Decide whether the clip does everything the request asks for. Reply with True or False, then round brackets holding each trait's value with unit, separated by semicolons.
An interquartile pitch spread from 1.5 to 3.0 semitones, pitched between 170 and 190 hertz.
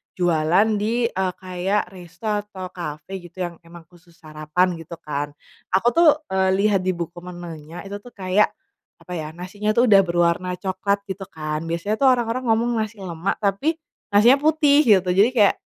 False (3.6 semitones; 185 Hz)